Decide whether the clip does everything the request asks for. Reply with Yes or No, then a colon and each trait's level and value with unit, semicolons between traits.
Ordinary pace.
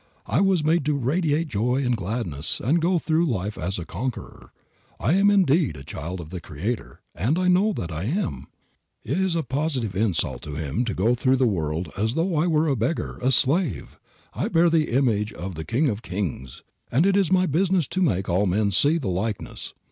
No: fast, 215 wpm